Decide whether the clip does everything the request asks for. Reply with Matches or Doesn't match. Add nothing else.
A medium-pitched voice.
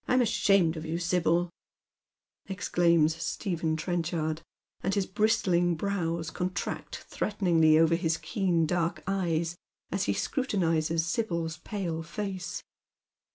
Matches